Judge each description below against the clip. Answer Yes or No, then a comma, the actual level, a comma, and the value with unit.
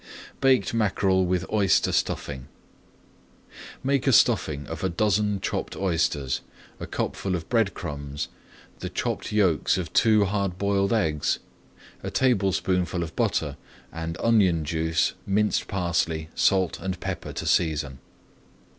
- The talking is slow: Yes, slow, 130 wpm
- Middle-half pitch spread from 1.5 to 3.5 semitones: No, average, 3.9 semitones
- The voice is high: No, very low, 95 Hz